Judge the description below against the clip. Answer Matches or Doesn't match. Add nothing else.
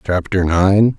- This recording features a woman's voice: Doesn't match